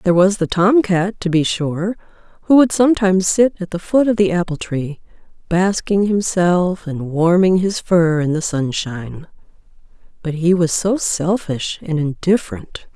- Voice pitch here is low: No, medium, 180 Hz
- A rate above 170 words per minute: No, average, 160 wpm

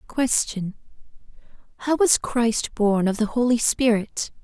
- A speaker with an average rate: No, slow, 110 wpm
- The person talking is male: No, female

